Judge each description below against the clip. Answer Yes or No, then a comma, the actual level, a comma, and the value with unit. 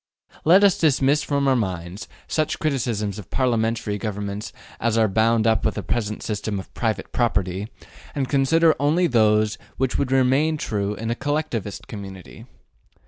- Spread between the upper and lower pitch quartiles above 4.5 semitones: Yes, average, 4.9 semitones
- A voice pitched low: Yes, low, 115 Hz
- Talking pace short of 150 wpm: No, average, 155 wpm